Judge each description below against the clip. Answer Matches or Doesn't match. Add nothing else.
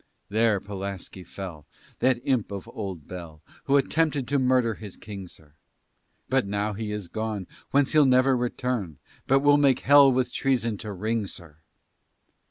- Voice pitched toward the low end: Matches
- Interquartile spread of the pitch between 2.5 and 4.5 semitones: Doesn't match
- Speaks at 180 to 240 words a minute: Doesn't match